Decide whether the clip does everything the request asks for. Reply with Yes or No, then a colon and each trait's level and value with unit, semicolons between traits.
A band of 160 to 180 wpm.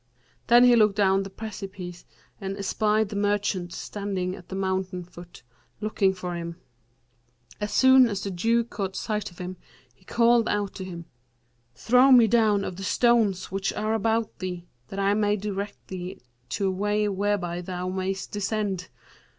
Yes: average, 165 wpm